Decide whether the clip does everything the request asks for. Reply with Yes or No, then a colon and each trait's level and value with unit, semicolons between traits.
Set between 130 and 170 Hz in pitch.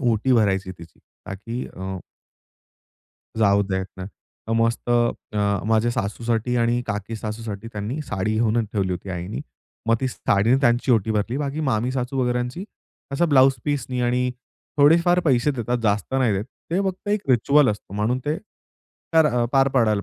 No: low, 120 Hz